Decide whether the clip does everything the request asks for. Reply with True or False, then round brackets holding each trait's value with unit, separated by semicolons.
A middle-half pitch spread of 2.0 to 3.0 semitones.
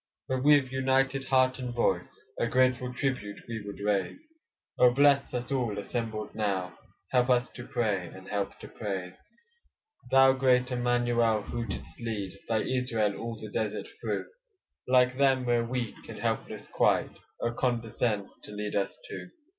False (3.5 semitones)